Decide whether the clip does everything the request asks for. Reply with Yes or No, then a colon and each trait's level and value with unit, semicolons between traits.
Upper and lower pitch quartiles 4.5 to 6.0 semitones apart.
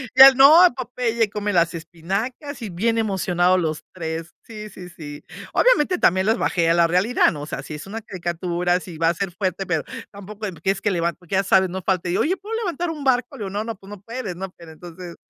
Yes: average, 4.8 semitones